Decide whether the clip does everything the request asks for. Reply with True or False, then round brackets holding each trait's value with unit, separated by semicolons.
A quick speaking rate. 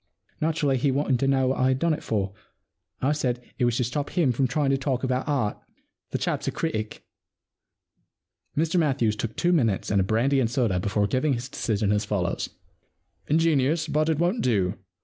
True (210 wpm)